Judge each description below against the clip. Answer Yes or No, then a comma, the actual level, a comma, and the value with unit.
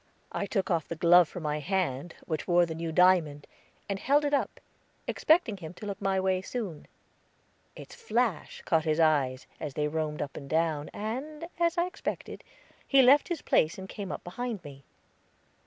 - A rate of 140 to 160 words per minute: No, average, 185 wpm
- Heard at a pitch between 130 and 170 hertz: No, medium, 180 Hz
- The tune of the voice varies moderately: No, wide, 6.6 semitones